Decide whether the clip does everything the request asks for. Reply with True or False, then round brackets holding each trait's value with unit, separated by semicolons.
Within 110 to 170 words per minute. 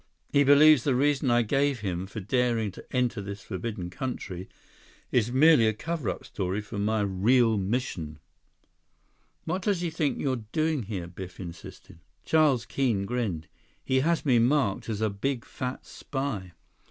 True (160 wpm)